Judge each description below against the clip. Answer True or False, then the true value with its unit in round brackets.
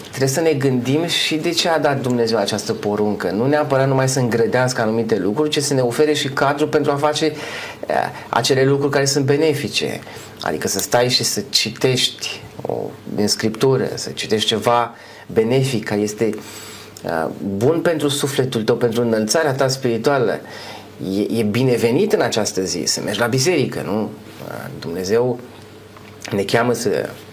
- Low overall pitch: True (125 Hz)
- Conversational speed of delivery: True (160 wpm)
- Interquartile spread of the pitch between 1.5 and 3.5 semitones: False (4.6 semitones)